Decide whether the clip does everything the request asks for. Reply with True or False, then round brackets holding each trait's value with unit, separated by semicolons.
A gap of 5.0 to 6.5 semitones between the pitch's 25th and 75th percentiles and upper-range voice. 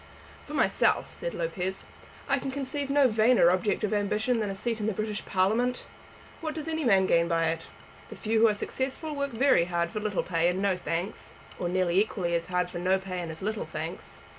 True (5.6 semitones; 205 Hz)